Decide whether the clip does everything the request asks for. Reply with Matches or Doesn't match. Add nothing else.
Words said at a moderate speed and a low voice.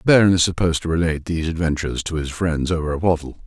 Doesn't match